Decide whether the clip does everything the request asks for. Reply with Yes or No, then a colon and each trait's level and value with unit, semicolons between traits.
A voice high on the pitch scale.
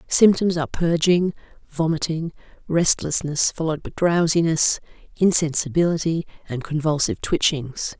No: medium, 160 Hz